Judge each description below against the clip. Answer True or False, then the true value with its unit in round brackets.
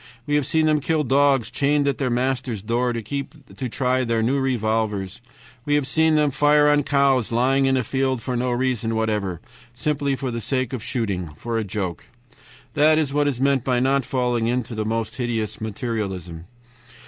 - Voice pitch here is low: True (125 Hz)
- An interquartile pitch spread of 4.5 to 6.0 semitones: False (3.7 semitones)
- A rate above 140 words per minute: True (185 wpm)